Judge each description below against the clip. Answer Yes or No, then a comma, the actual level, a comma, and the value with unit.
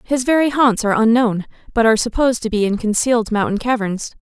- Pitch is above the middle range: Yes, high, 230 Hz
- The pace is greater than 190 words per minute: Yes, average, 200 wpm